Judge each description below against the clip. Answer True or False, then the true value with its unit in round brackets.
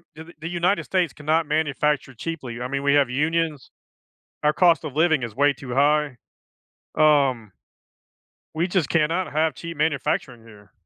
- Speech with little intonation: False (3.4 semitones)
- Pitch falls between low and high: True (150 Hz)